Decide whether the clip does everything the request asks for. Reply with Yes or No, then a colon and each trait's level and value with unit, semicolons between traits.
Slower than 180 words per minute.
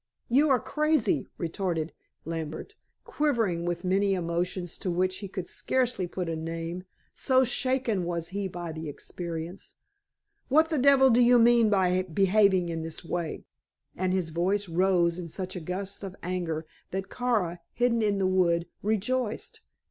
Yes: average, 155 wpm